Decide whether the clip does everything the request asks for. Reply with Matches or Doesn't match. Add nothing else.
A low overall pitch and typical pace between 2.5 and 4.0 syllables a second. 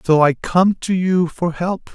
Doesn't match